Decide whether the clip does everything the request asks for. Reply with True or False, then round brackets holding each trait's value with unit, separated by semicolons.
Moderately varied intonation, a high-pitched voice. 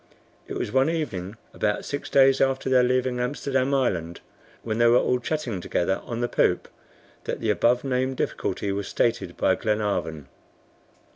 False (4.6 semitones; 120 Hz)